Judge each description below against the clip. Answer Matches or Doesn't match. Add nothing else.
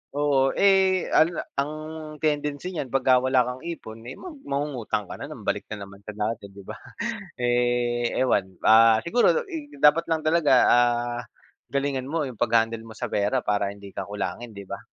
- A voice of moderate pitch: Doesn't match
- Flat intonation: Doesn't match